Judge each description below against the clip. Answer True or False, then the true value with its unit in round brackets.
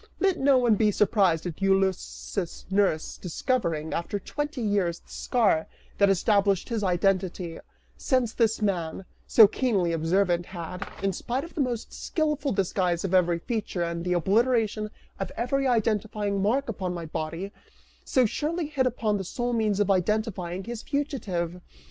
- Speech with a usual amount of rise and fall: True (4.9 semitones)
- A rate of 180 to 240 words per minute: False (155 wpm)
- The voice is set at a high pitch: True (200 Hz)